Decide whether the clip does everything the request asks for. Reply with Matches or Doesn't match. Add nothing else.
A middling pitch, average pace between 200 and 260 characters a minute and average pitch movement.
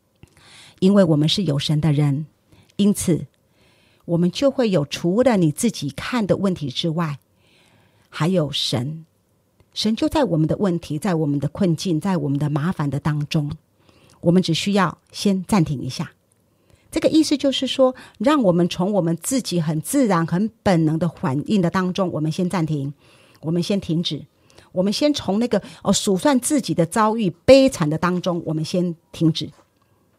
Matches